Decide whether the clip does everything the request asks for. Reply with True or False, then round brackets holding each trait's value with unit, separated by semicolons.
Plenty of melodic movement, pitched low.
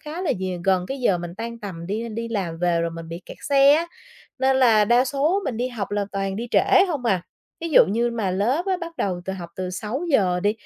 False (6.3 semitones; 220 Hz)